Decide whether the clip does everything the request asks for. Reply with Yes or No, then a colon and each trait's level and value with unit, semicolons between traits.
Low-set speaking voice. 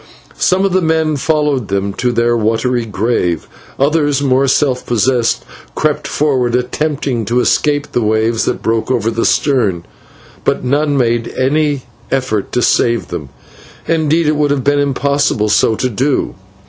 Yes: low, 130 Hz